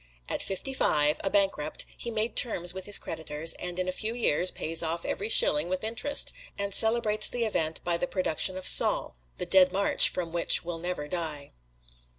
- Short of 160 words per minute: No, average, 190 wpm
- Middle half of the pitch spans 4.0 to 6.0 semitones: Yes, average, 4.5 semitones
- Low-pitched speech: No, medium, 185 Hz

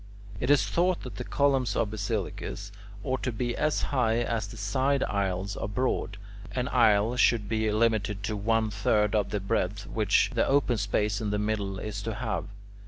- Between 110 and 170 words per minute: No, average, 185 wpm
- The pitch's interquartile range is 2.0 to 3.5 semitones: Yes, average, 3.2 semitones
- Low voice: Yes, low, 110 Hz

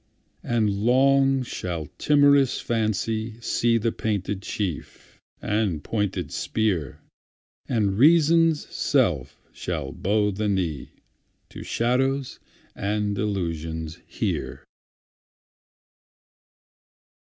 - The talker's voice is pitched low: Yes, low, 110 Hz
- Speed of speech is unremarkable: No, slow, 75 wpm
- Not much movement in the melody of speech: No, average, 4.7 semitones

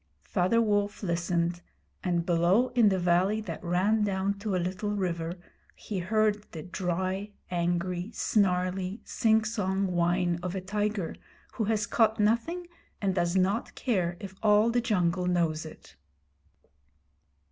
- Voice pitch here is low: No, high, 190 Hz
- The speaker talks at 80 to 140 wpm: Yes, slow, 135 wpm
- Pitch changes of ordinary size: Yes, average, 3.2 semitones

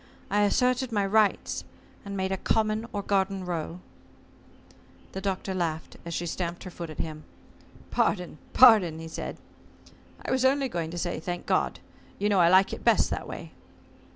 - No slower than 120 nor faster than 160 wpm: No, average, 175 wpm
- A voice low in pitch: No, high, 190 Hz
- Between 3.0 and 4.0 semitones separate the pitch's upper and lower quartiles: Yes, average, 3.3 semitones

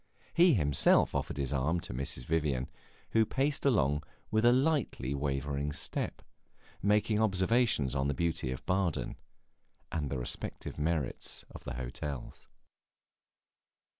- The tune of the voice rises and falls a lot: Yes, wide, 7.7 semitones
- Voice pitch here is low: Yes, very low, 75 Hz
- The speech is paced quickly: No, slow, 135 wpm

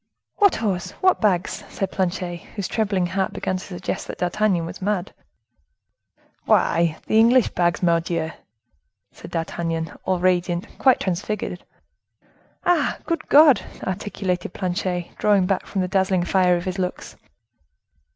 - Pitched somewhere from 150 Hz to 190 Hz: Yes, medium, 185 Hz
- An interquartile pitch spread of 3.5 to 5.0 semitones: No, average, 2.7 semitones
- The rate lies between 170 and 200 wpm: No, slow, 135 wpm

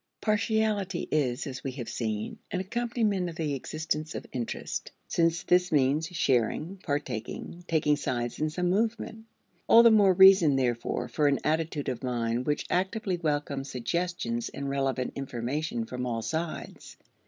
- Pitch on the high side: No, medium, 155 Hz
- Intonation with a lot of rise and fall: Yes, wide, 5.9 semitones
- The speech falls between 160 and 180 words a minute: No, average, 150 wpm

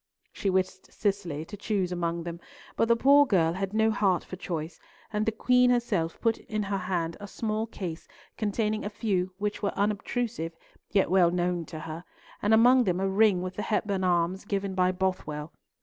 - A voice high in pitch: Yes, high, 195 Hz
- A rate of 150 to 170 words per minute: No, average, 190 wpm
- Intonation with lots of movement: No, average, 3.3 semitones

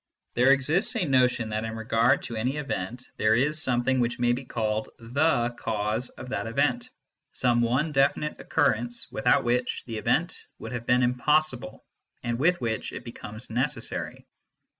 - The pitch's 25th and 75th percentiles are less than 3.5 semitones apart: Yes, average, 2.9 semitones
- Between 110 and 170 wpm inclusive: Yes, average, 165 wpm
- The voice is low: Yes, low, 125 Hz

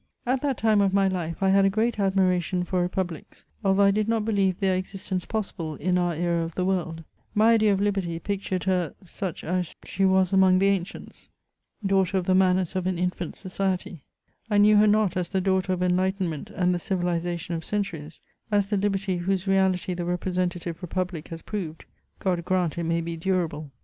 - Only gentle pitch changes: Yes, narrow, 1.9 semitones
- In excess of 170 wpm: Yes, average, 200 wpm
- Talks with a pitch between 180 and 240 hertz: Yes, medium, 185 Hz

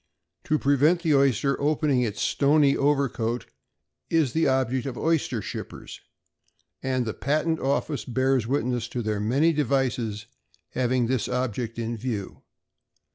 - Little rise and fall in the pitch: No, average, 3.3 semitones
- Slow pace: Yes, slow, 130 wpm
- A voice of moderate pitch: No, low, 130 Hz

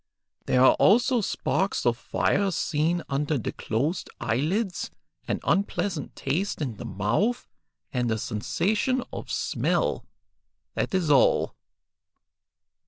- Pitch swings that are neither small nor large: No, wide, 8.0 semitones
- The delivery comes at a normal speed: No, slow, 115 wpm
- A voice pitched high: No, medium, 155 Hz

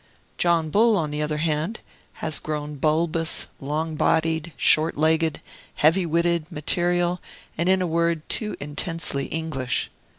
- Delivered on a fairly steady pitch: Yes, narrow, 2.0 semitones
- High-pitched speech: No, medium, 160 Hz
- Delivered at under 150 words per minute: Yes, slow, 135 wpm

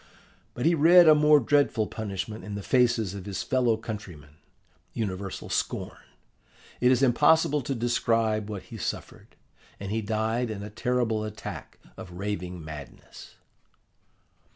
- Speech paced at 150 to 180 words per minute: No, average, 140 wpm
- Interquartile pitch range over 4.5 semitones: No, average, 3.8 semitones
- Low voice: Yes, low, 110 Hz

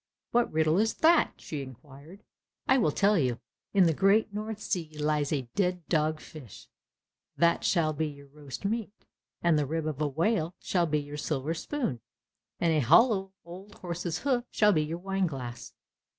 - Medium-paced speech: Yes, average, 180 wpm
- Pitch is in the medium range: Yes, medium, 165 Hz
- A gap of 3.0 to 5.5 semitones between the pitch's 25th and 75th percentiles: Yes, average, 4.8 semitones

